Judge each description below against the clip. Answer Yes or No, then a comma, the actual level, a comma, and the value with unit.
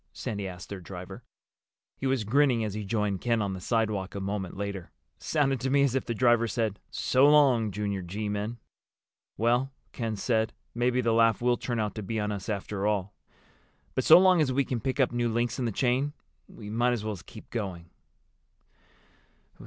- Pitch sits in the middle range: No, low, 110 Hz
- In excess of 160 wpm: Yes, average, 195 wpm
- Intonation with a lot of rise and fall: No, average, 3.4 semitones